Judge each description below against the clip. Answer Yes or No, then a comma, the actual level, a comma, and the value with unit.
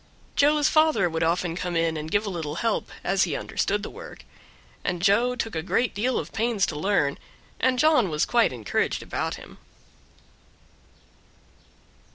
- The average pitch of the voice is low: No, high, 195 Hz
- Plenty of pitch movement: Yes, wide, 6.4 semitones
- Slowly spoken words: No, average, 165 wpm